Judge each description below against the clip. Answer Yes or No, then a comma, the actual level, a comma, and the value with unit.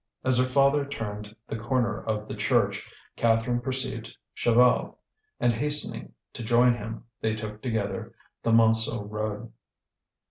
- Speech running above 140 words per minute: No, slow, 135 wpm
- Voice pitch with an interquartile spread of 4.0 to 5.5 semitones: No, narrow, 2.5 semitones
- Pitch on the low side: Yes, low, 115 Hz